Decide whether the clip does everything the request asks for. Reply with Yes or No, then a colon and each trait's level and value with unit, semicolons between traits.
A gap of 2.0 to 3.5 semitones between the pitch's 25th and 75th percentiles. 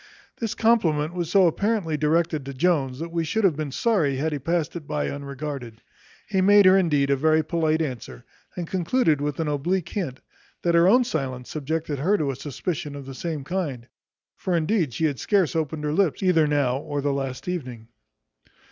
No: average, 4.1 semitones